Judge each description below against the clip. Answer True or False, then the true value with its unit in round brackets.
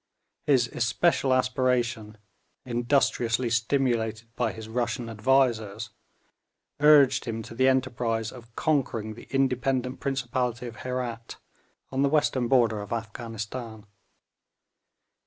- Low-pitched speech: True (120 Hz)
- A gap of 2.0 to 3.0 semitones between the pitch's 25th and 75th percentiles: True (2.5 semitones)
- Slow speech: True (105 wpm)